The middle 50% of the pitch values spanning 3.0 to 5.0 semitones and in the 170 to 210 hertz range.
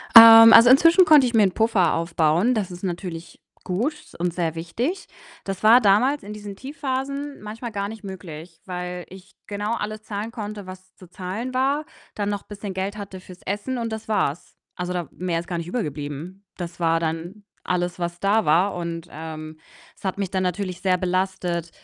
Yes: average, 4.0 semitones; high, 190 Hz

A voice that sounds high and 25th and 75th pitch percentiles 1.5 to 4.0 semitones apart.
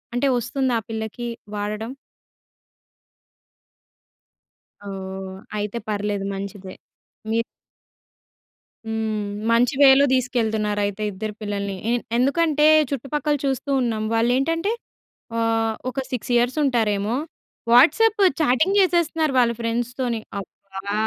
No: high, 230 Hz; average, 4.4 semitones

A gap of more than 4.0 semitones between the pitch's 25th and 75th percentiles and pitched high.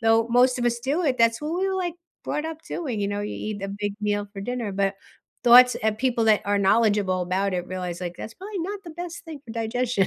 Yes: average, 4.5 semitones; high, 225 Hz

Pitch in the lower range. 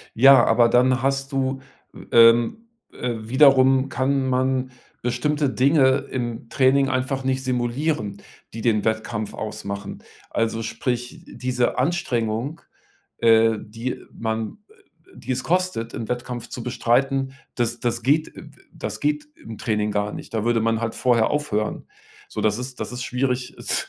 Yes: low, 125 Hz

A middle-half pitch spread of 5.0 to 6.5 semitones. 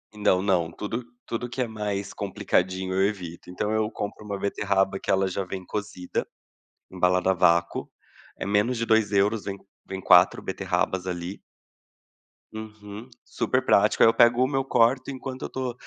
No: average, 3.2 semitones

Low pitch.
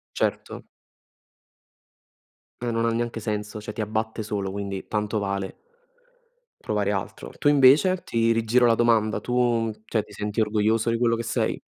Yes: low, 110 Hz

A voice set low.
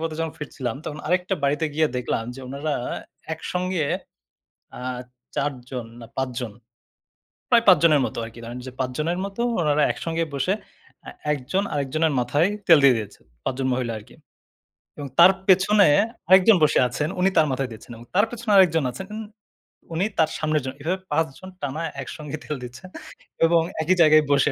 No: medium, 155 Hz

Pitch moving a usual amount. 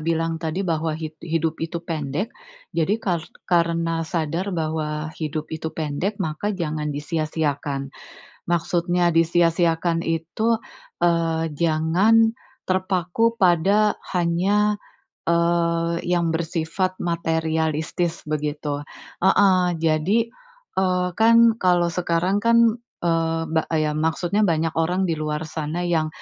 No: narrow, 2.2 semitones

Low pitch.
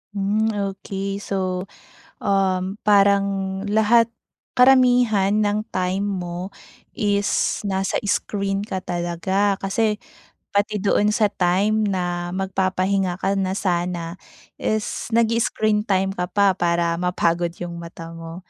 No: high, 195 Hz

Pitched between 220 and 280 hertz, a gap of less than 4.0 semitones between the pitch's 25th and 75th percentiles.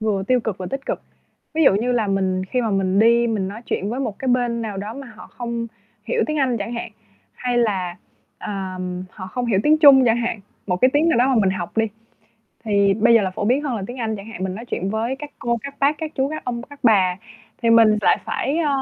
No: high, 230 Hz; average, 4.4 semitones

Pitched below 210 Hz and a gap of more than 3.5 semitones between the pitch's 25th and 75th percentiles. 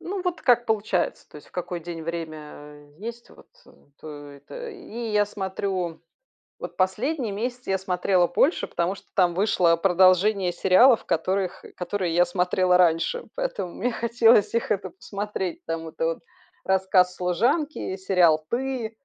Yes: high, 190 Hz; average, 4.5 semitones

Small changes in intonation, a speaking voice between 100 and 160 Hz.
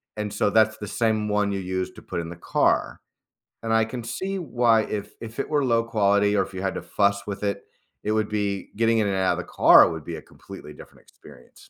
Yes: narrow, 2.3 semitones; low, 105 Hz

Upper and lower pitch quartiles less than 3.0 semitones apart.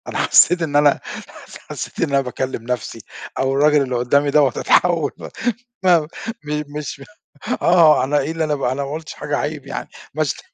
Yes: narrow, 2.6 semitones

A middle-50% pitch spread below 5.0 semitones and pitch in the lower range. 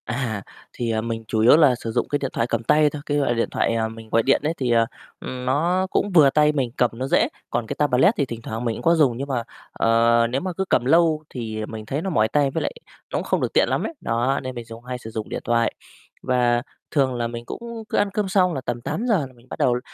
Yes: average, 4.3 semitones; low, 125 Hz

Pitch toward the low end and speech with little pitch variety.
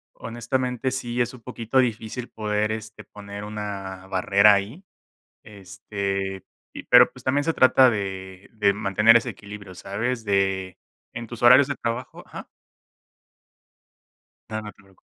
No: low, 105 Hz; average, 3.4 semitones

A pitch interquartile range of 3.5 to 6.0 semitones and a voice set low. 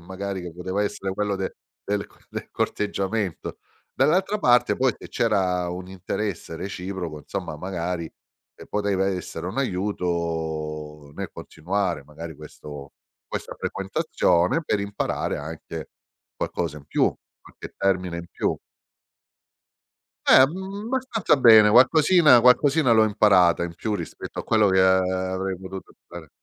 Yes: average, 4.0 semitones; very low, 95 Hz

